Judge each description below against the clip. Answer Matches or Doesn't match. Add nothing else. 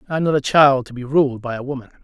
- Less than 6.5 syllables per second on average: Doesn't match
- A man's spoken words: Matches